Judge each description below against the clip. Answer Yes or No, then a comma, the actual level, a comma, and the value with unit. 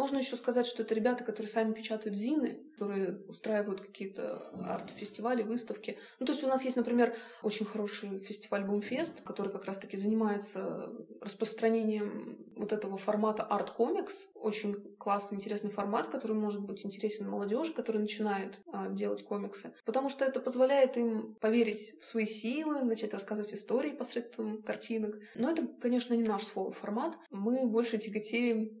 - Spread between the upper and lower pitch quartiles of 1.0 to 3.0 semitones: Yes, narrow, 2.6 semitones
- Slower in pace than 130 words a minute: No, average, 150 wpm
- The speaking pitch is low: No, high, 220 Hz